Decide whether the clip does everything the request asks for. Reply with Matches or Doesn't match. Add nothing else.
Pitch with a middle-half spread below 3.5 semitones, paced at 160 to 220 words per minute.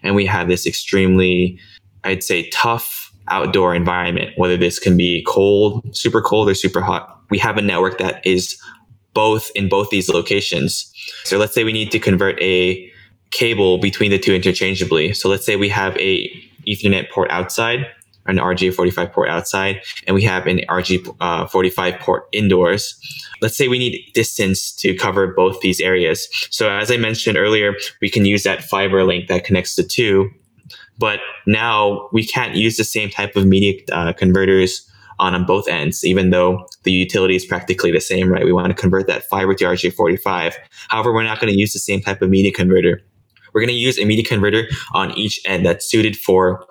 Matches